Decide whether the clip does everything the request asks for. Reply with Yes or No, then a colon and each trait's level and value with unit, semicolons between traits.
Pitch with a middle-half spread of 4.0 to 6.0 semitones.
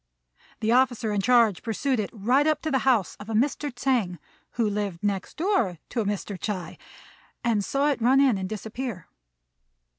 Yes: average, 4.4 semitones